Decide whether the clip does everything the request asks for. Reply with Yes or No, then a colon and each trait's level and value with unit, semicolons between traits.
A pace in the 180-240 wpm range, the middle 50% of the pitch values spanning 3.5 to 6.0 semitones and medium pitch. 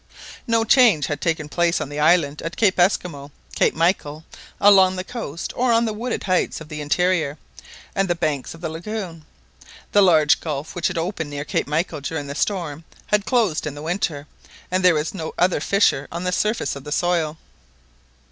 Yes: average, 195 wpm; average, 4.1 semitones; medium, 170 Hz